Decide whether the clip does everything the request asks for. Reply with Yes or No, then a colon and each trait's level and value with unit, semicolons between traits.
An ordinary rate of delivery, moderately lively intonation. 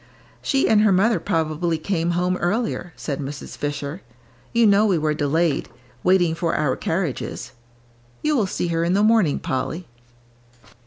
Yes: average, 155 wpm; average, 4.4 semitones